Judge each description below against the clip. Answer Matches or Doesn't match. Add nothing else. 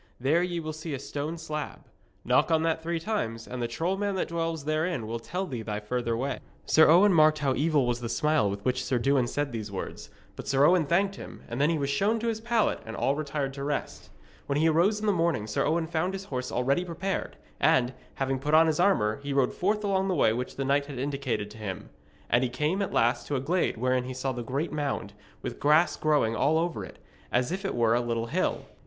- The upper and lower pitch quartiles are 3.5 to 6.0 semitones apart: Matches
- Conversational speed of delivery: Doesn't match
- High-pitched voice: Doesn't match